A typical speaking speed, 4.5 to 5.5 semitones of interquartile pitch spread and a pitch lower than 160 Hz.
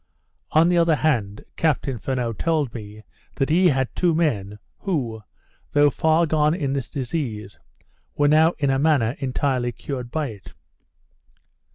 Yes: average, 150 wpm; average, 4.8 semitones; medium, 140 Hz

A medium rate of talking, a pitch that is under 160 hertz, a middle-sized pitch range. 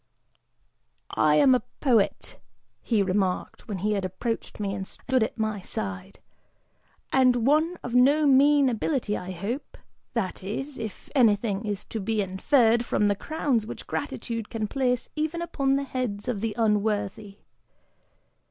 No: average, 150 wpm; high, 225 Hz; average, 4.5 semitones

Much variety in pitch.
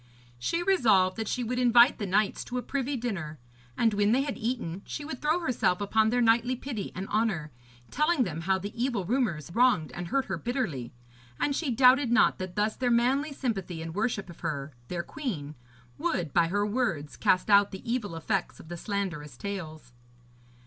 Yes: wide, 6.1 semitones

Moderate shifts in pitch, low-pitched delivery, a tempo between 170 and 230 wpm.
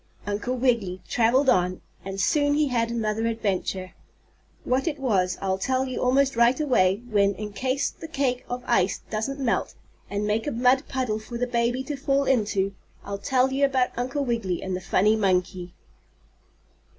No: average, 4.7 semitones; high, 235 Hz; average, 175 wpm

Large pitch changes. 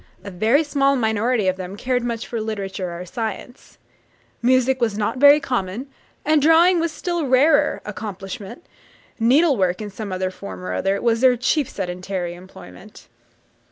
Yes: wide, 5.7 semitones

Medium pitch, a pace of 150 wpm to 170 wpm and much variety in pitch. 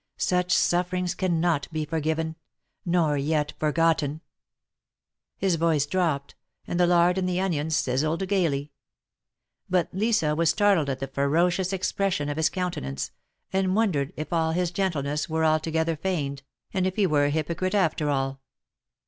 No: medium, 165 Hz; average, 155 wpm; average, 3.4 semitones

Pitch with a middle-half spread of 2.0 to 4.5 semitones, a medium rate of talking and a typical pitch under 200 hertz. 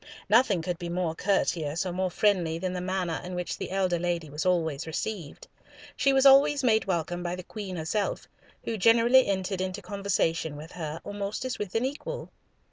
Yes: average, 3.4 semitones; average, 190 wpm; medium, 185 Hz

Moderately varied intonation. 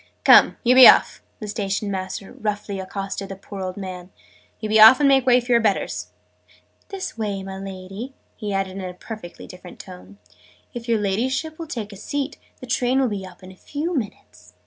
Yes: average, 4.3 semitones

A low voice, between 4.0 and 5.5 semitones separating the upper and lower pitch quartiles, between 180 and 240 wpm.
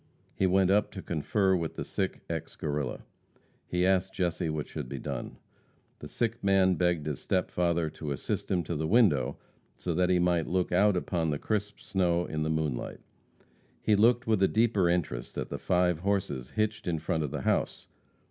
No: very low, 90 Hz; average, 3.6 semitones; average, 195 wpm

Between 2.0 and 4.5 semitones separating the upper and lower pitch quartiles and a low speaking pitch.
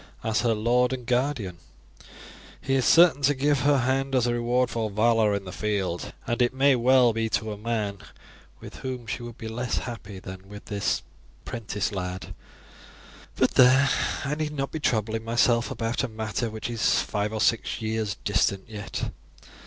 Yes: average, 3.3 semitones; low, 115 Hz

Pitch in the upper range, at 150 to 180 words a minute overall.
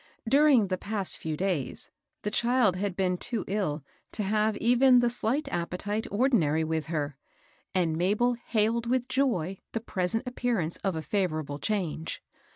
Yes: high, 205 Hz; average, 160 wpm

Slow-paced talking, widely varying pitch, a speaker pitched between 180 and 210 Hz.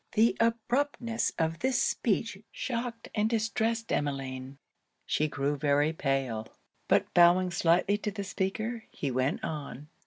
Yes: slow, 130 wpm; wide, 7.8 semitones; high, 190 Hz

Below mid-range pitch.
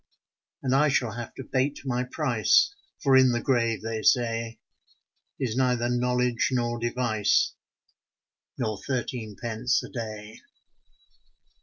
Yes: low, 120 Hz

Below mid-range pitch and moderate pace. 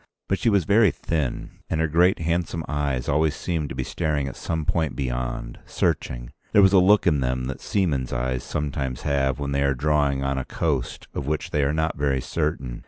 No: very low, 75 Hz; fast, 210 wpm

